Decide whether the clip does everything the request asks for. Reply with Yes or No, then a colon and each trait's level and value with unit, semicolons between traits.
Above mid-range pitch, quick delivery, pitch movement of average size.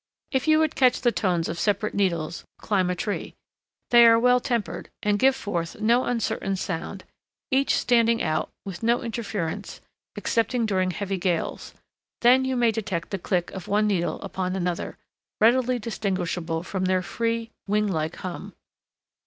No: high, 205 Hz; average, 160 wpm; average, 4.4 semitones